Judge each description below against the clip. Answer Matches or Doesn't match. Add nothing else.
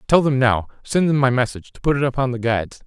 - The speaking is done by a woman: Doesn't match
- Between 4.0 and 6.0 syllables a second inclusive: Doesn't match